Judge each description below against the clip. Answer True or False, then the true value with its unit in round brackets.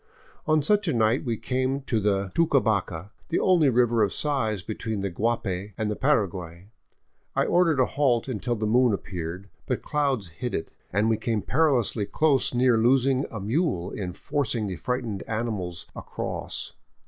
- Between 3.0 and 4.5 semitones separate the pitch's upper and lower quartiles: False (4.9 semitones)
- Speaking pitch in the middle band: False (115 Hz)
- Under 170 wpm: True (160 wpm)